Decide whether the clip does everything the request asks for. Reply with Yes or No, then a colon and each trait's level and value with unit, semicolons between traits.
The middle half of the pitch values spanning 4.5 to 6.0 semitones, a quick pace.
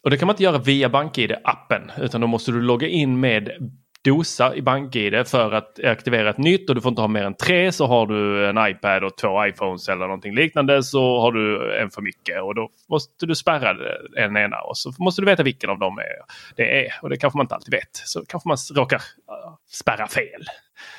Yes: wide, 5.5 semitones; fast, 225 wpm